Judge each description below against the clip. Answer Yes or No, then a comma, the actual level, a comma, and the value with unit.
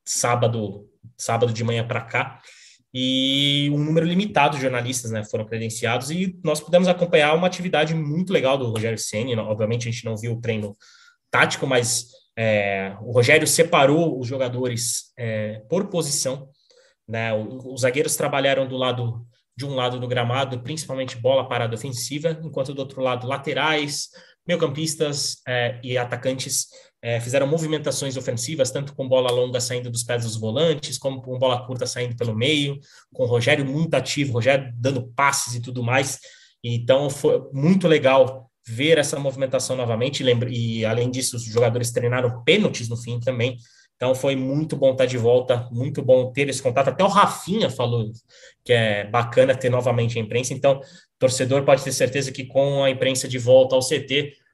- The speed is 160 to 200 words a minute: Yes, average, 170 wpm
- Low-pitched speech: Yes, low, 130 Hz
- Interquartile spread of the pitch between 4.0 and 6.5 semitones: No, average, 3.0 semitones